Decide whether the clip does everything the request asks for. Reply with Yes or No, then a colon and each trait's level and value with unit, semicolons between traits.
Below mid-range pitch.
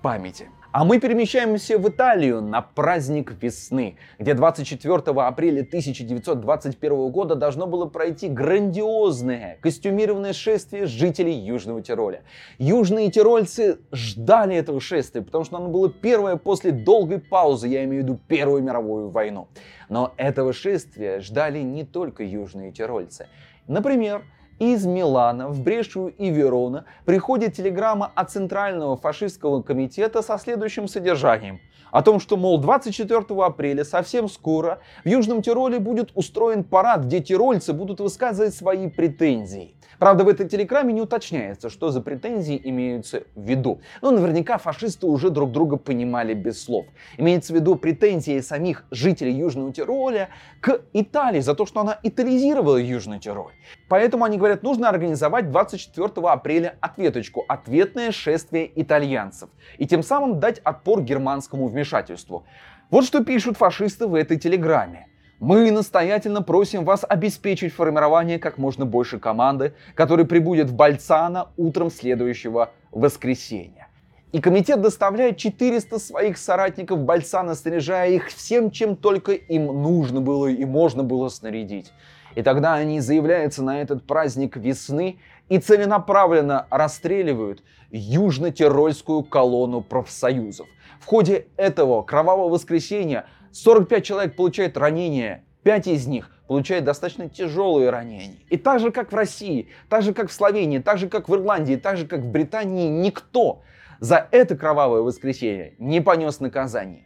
No: medium, 170 Hz